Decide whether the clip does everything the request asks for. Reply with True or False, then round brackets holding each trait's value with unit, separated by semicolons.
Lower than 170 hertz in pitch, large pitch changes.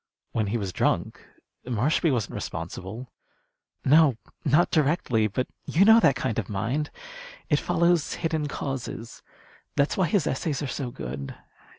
True (135 Hz; 5.9 semitones)